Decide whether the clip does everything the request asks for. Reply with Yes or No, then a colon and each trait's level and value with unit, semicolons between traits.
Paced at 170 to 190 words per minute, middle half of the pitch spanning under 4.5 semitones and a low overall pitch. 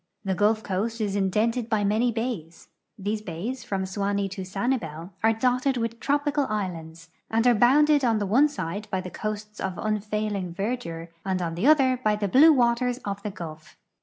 No: average, 180 wpm; average, 4.1 semitones; high, 210 Hz